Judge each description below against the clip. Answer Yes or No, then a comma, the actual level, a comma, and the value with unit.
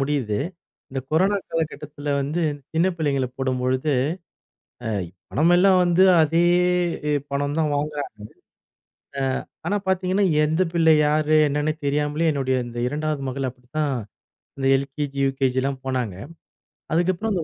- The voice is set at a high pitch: No, medium, 150 Hz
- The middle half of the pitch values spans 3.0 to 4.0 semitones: Yes, average, 3.4 semitones